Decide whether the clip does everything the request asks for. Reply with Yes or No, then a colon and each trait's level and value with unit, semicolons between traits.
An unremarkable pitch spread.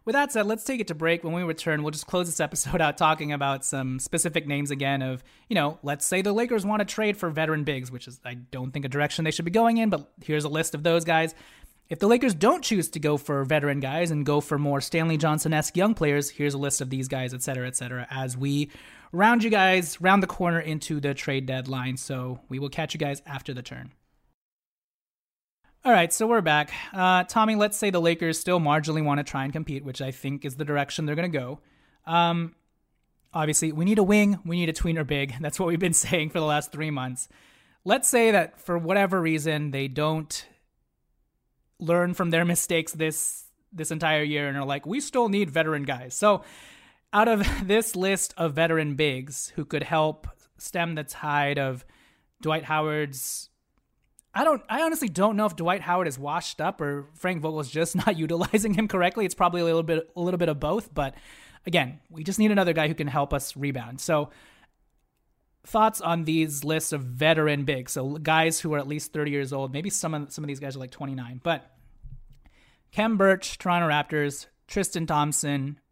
Yes: average, 3.8 semitones